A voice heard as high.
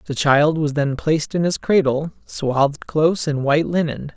No: medium, 150 Hz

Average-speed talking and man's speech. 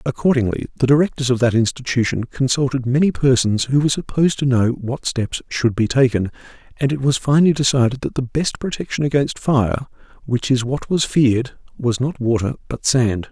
Yes: average, 170 wpm; male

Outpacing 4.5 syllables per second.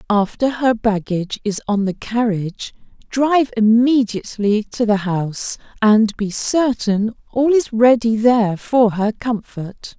No: 4.2 syllables/s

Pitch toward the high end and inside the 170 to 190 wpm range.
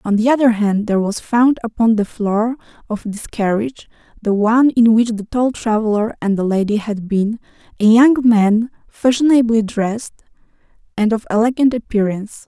No: high, 225 Hz; average, 155 wpm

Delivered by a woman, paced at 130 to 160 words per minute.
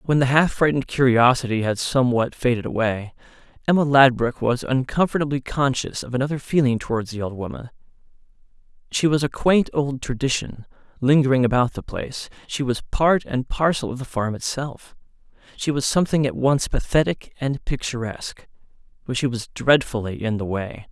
No: male; average, 155 wpm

